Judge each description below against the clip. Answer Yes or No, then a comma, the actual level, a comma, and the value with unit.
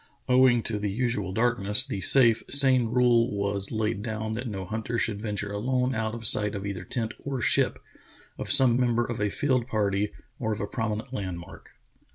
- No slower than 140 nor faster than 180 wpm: No, average, 190 wpm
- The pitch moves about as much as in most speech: Yes, average, 3.0 semitones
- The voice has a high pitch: No, low, 110 Hz